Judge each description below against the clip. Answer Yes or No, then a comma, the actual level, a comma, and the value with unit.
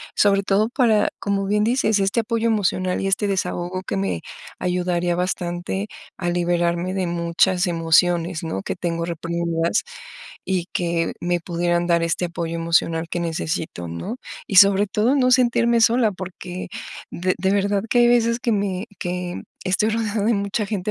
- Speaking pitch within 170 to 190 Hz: Yes, medium, 185 Hz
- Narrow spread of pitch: No, average, 3.2 semitones